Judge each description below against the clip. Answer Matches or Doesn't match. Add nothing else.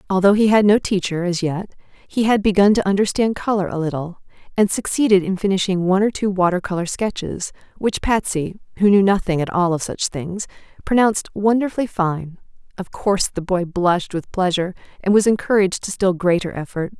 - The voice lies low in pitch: Doesn't match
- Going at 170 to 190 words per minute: Matches